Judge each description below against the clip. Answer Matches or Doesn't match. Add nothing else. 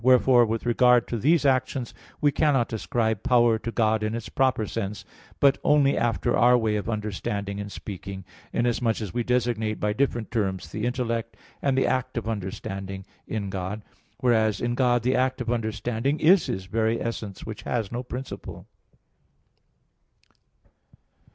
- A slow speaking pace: Doesn't match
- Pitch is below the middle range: Matches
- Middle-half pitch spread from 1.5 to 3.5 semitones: Matches